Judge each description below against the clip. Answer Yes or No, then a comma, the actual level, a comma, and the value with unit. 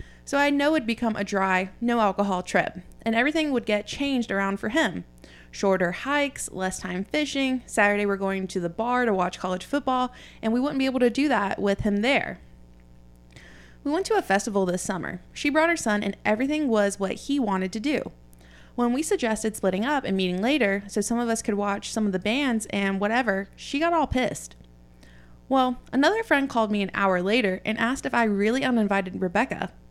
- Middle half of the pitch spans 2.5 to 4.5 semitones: No, average, 5.2 semitones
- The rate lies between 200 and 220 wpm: Yes, fast, 205 wpm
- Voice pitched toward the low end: No, high, 210 Hz